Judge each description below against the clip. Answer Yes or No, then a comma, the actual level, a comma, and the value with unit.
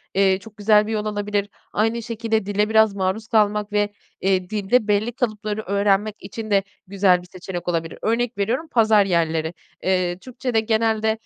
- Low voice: No, high, 210 Hz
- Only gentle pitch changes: Yes, narrow, 2.2 semitones